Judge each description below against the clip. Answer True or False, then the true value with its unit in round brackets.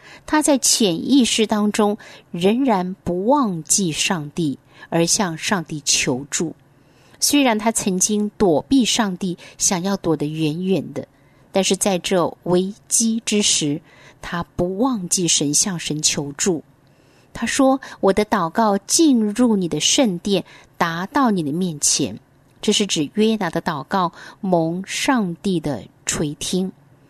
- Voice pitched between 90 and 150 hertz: False (185 Hz)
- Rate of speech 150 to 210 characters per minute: True (190 characters per minute)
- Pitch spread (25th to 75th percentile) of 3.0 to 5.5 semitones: True (5.1 semitones)